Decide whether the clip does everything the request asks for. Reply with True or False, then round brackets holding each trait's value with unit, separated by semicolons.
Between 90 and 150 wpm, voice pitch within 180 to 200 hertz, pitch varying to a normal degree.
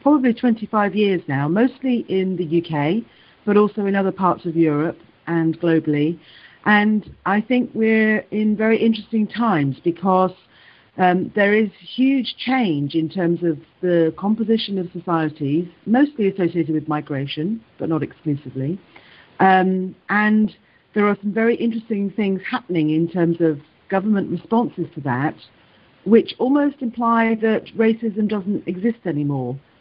True (140 wpm; 190 Hz; 5.0 semitones)